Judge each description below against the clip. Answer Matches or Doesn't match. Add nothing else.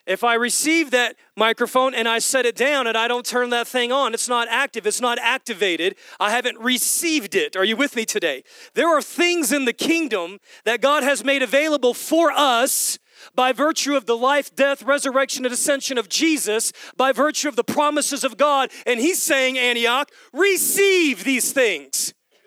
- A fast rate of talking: Doesn't match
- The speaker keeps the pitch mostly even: Doesn't match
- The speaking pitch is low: Doesn't match